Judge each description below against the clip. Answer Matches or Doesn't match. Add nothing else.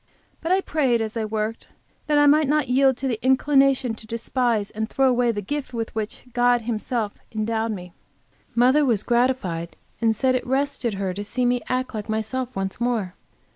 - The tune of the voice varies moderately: Matches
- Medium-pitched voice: Doesn't match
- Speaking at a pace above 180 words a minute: Matches